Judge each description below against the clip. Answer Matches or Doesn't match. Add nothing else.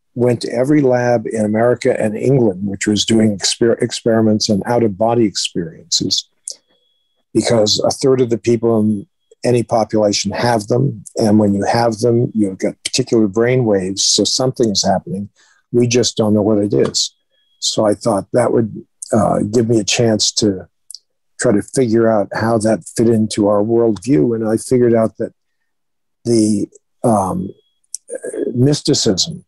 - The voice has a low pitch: Matches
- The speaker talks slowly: Doesn't match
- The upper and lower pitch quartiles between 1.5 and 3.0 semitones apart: Matches